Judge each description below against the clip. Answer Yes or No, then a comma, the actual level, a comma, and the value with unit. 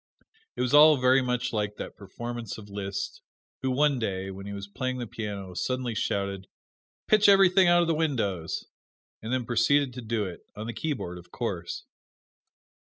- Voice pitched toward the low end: Yes, low, 120 Hz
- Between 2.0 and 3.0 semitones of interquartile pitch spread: No, average, 4.9 semitones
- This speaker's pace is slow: No, average, 175 wpm